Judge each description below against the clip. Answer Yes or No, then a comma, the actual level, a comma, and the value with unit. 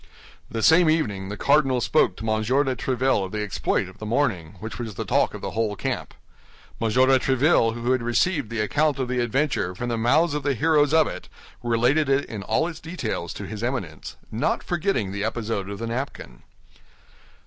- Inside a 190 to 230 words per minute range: Yes, fast, 205 wpm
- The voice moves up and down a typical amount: Yes, average, 5.0 semitones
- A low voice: Yes, low, 120 Hz